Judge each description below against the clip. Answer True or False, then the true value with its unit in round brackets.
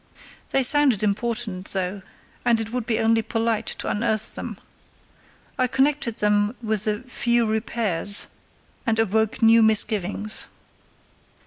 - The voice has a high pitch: True (220 Hz)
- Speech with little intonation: True (2.2 semitones)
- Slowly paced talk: True (125 wpm)